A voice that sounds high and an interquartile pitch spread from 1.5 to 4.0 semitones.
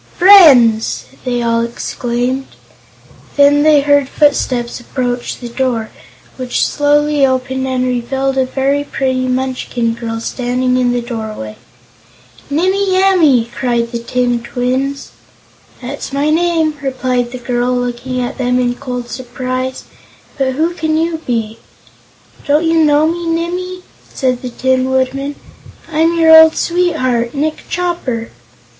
Yes: very high, 260 Hz; average, 3.4 semitones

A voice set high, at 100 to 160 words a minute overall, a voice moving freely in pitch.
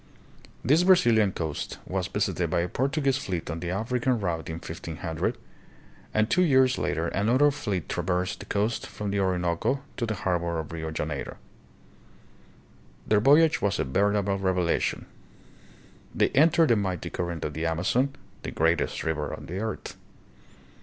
No: very low, 95 Hz; average, 155 wpm; wide, 6.5 semitones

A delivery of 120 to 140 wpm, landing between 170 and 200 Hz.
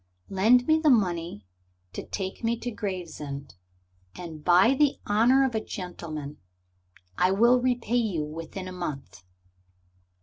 Yes: slow, 135 wpm; high, 190 Hz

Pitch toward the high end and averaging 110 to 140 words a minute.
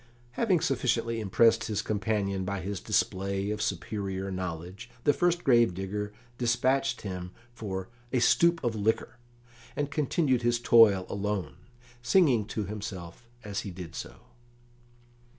No: low, 105 Hz; slow, 135 wpm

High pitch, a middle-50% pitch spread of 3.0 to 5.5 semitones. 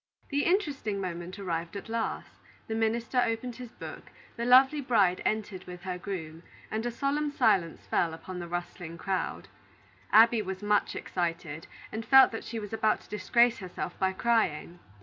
Yes: high, 210 Hz; average, 4.7 semitones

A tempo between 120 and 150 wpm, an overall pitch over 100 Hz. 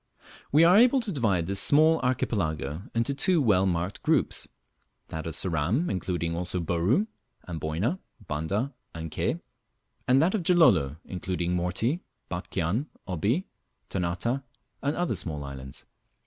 No: slow, 135 wpm; very low, 95 Hz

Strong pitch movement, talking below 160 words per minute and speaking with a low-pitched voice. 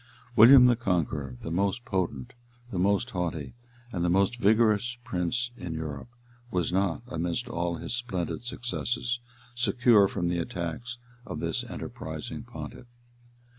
Yes: wide, 5.7 semitones; average, 140 wpm; low, 100 Hz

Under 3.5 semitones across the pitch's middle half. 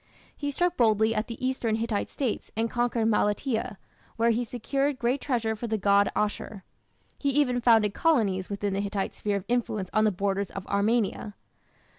Yes: average, 3.1 semitones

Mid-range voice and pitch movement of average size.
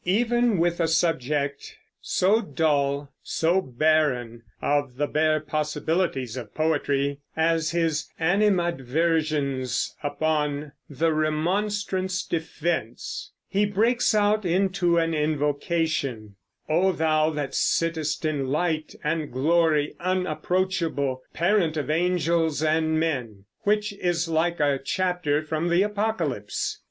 Yes: medium, 160 Hz; average, 3.3 semitones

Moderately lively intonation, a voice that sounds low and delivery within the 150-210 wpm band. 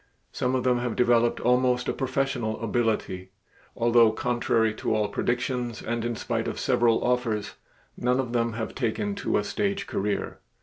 No: narrow, 2.0 semitones; low, 120 Hz; average, 165 wpm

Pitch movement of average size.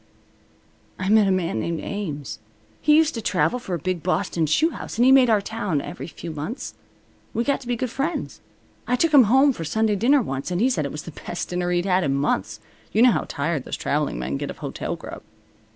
No: wide, 7.7 semitones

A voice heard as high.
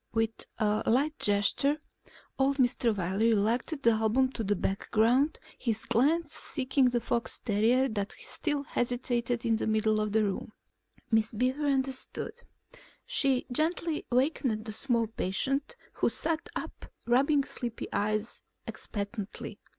Yes: high, 240 Hz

